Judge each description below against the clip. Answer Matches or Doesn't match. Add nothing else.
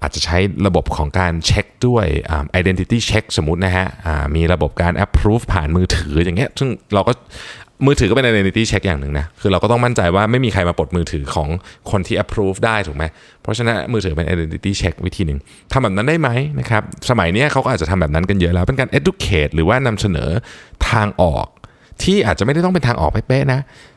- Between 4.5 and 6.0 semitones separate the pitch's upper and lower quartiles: Matches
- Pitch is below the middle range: Matches